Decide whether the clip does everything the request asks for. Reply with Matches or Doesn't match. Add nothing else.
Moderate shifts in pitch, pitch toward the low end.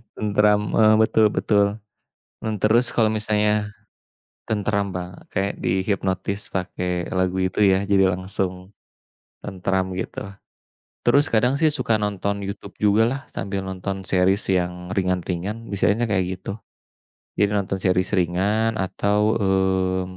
Doesn't match